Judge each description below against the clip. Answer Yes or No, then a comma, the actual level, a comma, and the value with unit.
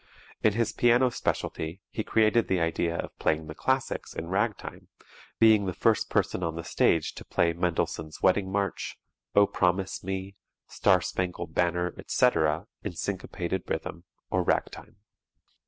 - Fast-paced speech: No, average, 145 wpm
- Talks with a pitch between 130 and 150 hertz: No, very low, 95 Hz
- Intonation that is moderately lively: Yes, average, 3.5 semitones